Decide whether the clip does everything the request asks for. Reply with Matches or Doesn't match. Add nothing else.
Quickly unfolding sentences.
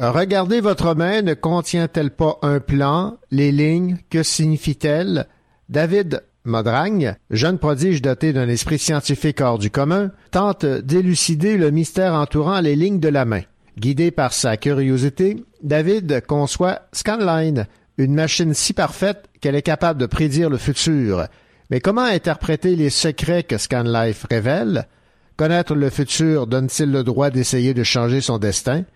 Doesn't match